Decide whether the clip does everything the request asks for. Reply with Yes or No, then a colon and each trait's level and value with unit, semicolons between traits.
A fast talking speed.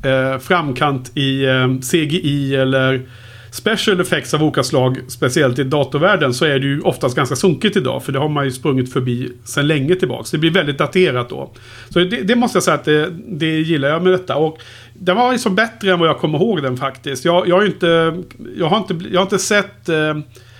Yes: fast, 215 wpm